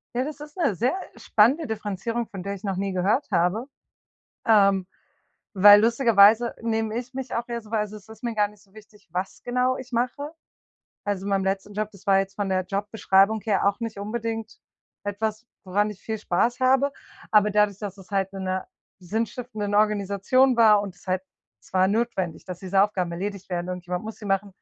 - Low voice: No, high, 210 Hz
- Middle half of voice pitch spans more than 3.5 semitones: No, average, 2.8 semitones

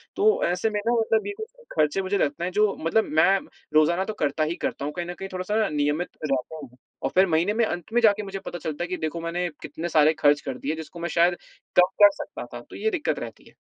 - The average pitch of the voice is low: No, medium, 175 Hz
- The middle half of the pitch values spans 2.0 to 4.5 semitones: No, average, 5.1 semitones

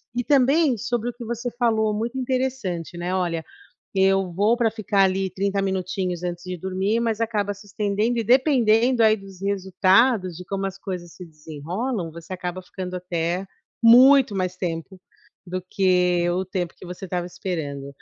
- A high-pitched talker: Yes, high, 195 Hz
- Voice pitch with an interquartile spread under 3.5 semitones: No, average, 4.1 semitones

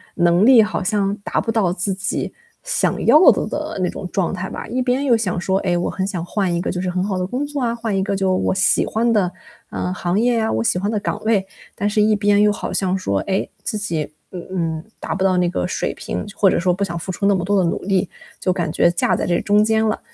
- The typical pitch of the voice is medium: No, high, 195 Hz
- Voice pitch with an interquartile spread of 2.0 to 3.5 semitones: Yes, average, 2.9 semitones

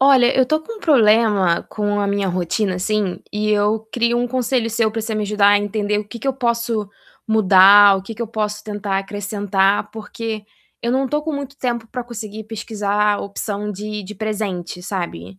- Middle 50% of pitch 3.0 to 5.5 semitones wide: No, narrow, 2.5 semitones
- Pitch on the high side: Yes, high, 210 Hz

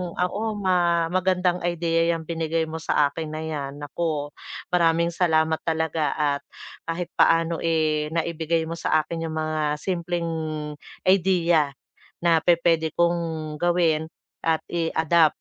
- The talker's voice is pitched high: No, medium, 165 Hz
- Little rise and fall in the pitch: Yes, narrow, 1.5 semitones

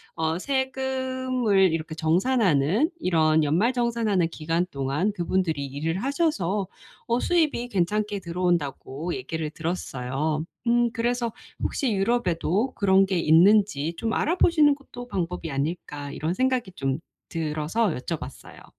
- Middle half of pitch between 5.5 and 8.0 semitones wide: Yes, wide, 6.9 semitones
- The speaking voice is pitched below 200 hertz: Yes, medium, 185 Hz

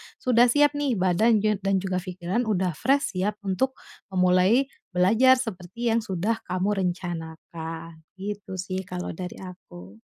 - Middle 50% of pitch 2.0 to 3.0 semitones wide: No, average, 4.0 semitones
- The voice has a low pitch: No, high, 190 Hz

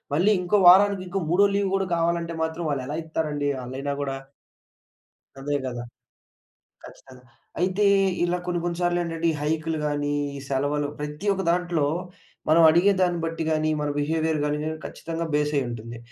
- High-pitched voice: No, medium, 160 Hz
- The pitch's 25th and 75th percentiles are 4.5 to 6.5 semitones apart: No, average, 3.2 semitones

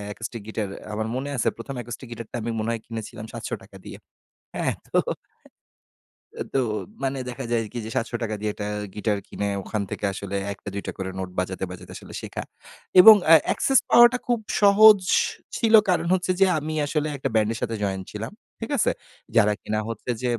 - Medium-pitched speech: No, low, 115 Hz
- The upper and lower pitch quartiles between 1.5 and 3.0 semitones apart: No, average, 5.3 semitones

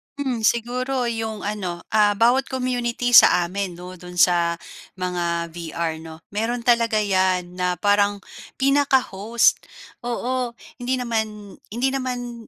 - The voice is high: Yes, high, 220 Hz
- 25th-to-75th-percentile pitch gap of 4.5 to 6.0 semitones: Yes, average, 5.2 semitones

